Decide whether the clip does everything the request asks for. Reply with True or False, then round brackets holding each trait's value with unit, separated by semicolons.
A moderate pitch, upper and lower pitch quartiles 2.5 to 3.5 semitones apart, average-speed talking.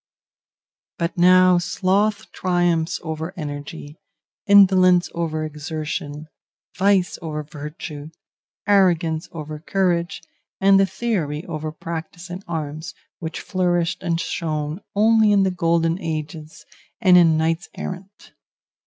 False (170 Hz; 2.9 semitones; 110 wpm)